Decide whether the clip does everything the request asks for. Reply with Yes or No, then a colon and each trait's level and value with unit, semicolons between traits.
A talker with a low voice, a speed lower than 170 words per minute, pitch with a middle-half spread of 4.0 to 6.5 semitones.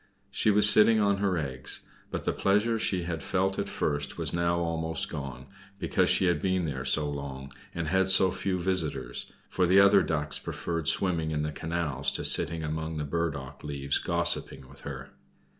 No: very low, 80 Hz; average, 185 wpm; average, 4.4 semitones